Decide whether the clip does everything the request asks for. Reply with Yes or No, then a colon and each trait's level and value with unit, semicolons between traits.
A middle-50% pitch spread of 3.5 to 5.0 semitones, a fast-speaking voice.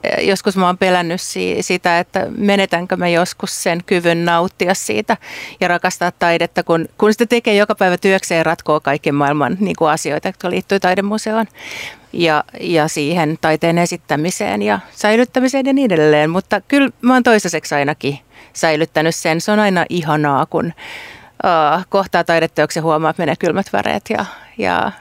Yes: average, 3.8 semitones; fast, 160 wpm